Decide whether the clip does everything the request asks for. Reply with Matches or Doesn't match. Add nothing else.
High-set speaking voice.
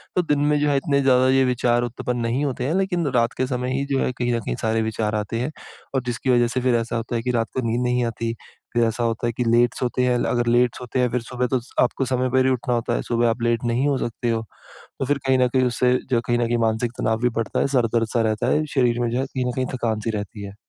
Doesn't match